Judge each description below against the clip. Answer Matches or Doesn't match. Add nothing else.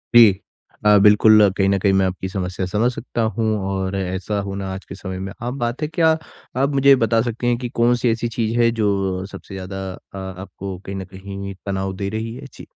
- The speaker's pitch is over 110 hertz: Doesn't match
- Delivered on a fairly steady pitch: Doesn't match